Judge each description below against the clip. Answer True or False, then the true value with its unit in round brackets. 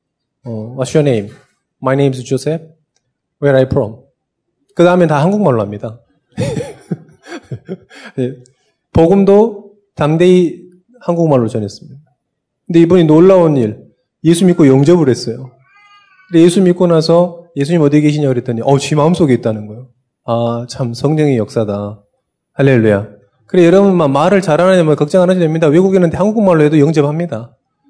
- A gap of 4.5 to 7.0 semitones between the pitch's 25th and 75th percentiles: True (5.4 semitones)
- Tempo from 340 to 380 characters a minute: True (365 characters per minute)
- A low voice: False (150 Hz)